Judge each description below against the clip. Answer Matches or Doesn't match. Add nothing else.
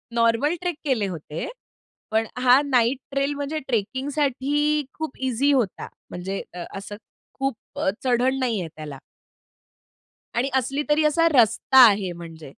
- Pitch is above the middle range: Matches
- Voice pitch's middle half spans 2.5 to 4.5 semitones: Doesn't match